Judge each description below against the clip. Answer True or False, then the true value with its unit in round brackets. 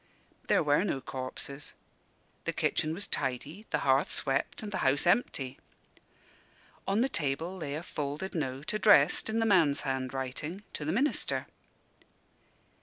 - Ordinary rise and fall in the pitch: False (5.9 semitones)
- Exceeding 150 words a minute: False (140 wpm)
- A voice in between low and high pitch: True (150 Hz)